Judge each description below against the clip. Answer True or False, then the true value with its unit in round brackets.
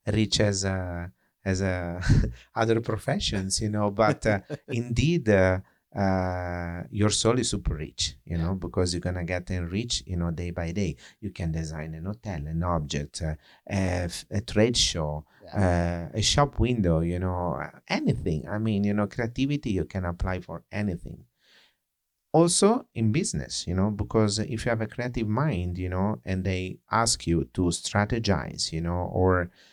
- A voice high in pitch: False (95 Hz)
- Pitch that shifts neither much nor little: True (3.8 semitones)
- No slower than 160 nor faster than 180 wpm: True (170 wpm)